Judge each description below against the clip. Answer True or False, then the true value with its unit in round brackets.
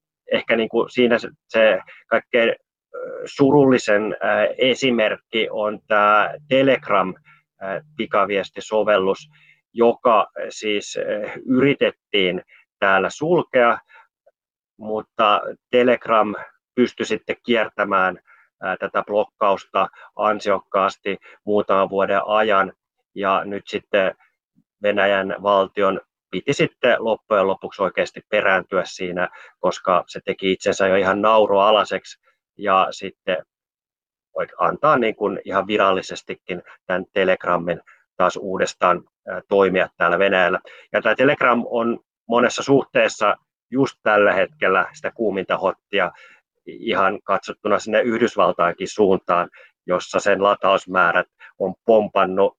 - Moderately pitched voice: False (110 Hz)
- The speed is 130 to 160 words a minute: False (95 wpm)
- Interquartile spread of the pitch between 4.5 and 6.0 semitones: True (4.9 semitones)